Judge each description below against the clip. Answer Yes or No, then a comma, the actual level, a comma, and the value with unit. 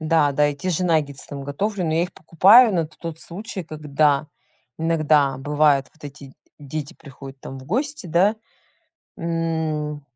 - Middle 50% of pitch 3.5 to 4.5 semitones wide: No, average, 2.8 semitones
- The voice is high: No, medium, 155 Hz